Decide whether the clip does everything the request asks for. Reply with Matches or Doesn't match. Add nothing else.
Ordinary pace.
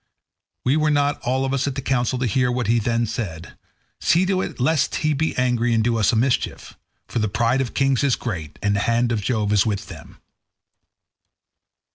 Doesn't match